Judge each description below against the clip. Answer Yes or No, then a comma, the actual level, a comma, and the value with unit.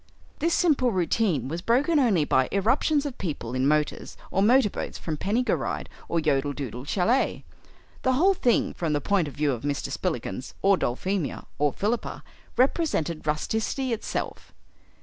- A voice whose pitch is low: No, medium, 185 Hz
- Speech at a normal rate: Yes, average, 165 wpm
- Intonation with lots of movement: Yes, wide, 9.0 semitones